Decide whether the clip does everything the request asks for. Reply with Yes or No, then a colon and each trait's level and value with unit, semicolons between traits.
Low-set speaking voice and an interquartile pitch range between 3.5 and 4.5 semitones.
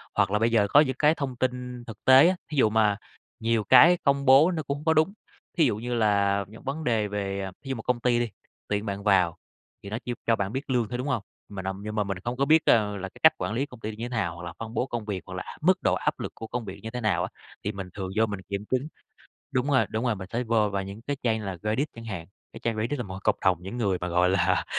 Yes: low, 110 Hz; average, 4.2 semitones